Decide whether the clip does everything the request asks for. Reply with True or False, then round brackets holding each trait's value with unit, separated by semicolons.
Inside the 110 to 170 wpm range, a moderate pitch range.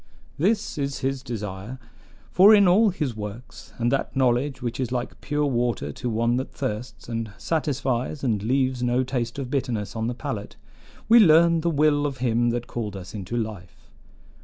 False (180 wpm; 3.7 semitones)